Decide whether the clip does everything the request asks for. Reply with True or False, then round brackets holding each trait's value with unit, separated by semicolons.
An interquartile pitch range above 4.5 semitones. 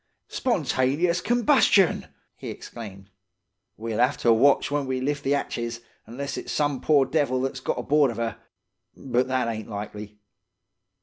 False (3.9 semitones)